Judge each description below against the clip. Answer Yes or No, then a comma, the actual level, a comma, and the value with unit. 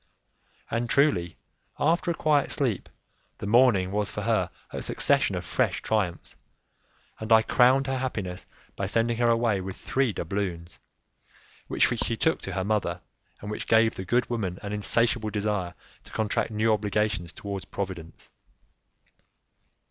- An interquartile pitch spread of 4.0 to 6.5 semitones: No, average, 3.6 semitones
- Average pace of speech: Yes, average, 150 wpm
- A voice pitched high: No, low, 110 Hz